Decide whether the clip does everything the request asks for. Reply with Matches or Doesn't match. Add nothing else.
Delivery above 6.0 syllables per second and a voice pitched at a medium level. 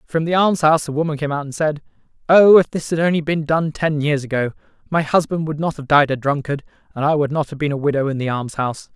Matches